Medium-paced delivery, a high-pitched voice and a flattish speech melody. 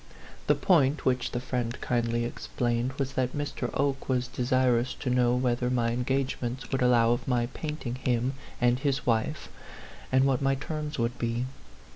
No: average, 170 wpm; low, 125 Hz; narrow, 1.9 semitones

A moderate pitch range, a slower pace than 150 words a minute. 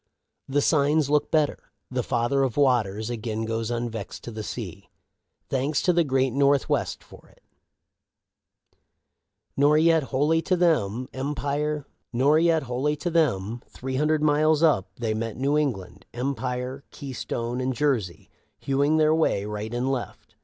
Yes: average, 4.0 semitones; slow, 135 wpm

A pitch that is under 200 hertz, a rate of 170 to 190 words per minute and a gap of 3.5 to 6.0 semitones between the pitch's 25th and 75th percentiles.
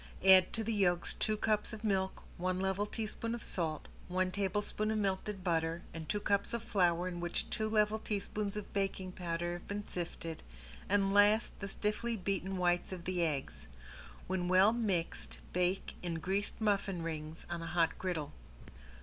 No: high, 190 Hz; average, 175 wpm; average, 3.0 semitones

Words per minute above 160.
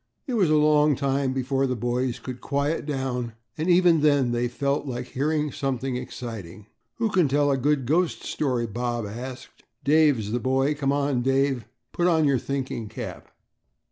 Yes: average, 170 wpm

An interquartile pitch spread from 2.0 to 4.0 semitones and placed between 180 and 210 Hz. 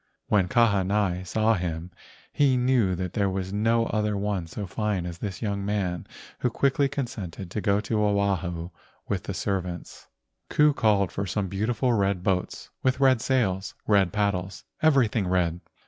No: average, 3.3 semitones; low, 100 Hz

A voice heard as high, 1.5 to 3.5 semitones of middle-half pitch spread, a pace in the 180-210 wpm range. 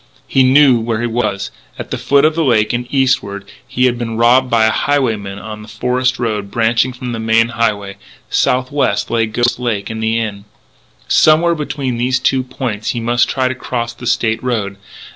No: low, 120 Hz; narrow, 2.6 semitones; average, 195 wpm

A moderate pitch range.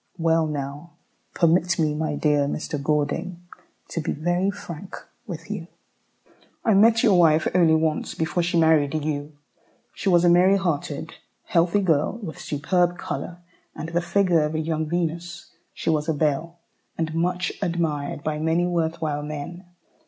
No: narrow, 2.3 semitones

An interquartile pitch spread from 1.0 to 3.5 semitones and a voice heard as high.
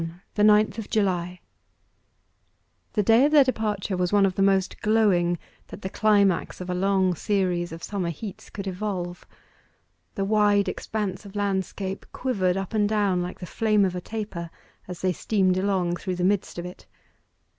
Yes: narrow, 2.5 semitones; high, 195 Hz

